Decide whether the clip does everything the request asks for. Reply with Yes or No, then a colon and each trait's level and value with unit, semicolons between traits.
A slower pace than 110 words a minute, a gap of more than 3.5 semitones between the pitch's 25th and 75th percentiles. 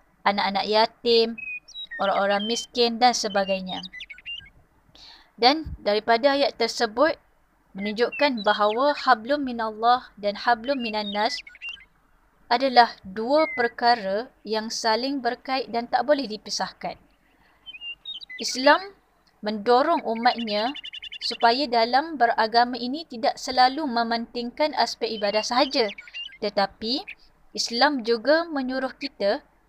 Yes: slow, 90 wpm; average, 4.0 semitones